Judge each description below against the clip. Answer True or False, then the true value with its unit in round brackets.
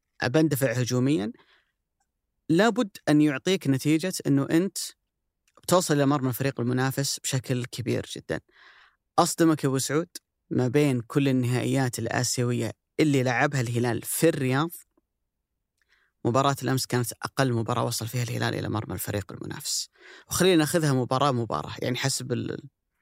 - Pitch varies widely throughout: False (3.5 semitones)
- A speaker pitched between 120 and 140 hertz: True (135 Hz)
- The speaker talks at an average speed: True (120 wpm)